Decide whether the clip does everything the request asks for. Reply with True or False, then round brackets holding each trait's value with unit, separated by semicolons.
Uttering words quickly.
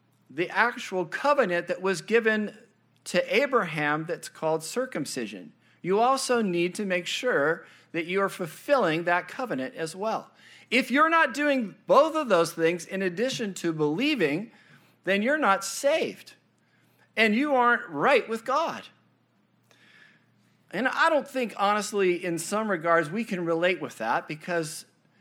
False (145 wpm)